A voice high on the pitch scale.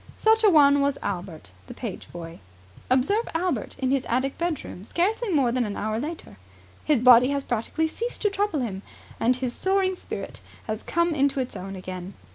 Yes: very high, 265 Hz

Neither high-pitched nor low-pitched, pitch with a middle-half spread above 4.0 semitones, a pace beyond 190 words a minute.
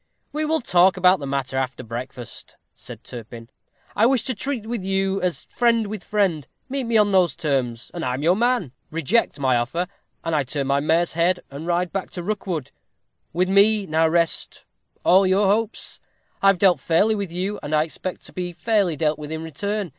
Yes: medium, 175 Hz; average, 5.2 semitones; average, 200 wpm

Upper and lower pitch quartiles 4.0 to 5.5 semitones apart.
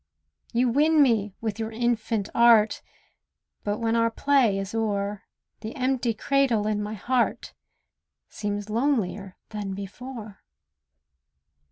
No: average, 2.8 semitones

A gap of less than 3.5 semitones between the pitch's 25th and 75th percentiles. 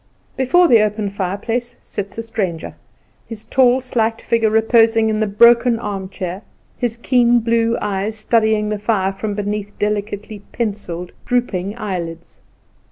Yes: narrow, 2.4 semitones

